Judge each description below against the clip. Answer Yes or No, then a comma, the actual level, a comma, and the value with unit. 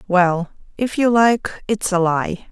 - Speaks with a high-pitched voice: Yes, high, 195 Hz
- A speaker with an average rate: Yes, average, 165 wpm